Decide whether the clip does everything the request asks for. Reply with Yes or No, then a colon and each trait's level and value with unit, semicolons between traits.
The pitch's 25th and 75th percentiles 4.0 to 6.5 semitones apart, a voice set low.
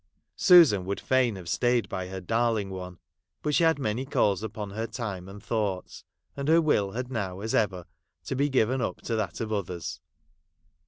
Yes: average, 4.8 semitones; low, 110 Hz